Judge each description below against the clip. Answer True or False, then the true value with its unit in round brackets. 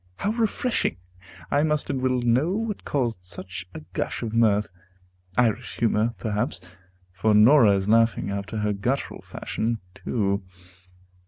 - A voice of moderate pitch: False (115 Hz)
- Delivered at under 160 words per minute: True (140 wpm)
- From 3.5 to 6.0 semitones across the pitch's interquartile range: True (3.9 semitones)